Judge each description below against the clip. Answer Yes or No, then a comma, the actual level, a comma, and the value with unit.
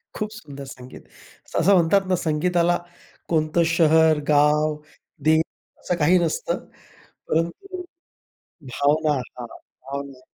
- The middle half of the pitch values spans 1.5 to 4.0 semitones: Yes, average, 2.9 semitones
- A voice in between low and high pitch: Yes, medium, 155 Hz